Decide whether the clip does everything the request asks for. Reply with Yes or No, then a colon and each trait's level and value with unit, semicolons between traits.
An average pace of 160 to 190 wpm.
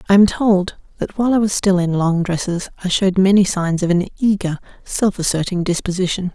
No: average, 200 wpm